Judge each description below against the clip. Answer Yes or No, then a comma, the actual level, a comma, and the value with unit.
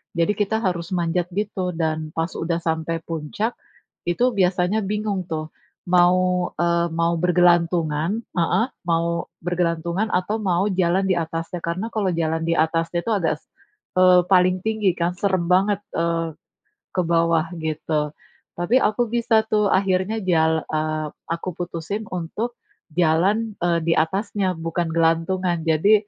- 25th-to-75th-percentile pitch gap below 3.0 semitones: Yes, narrow, 2.5 semitones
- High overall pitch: No, medium, 175 Hz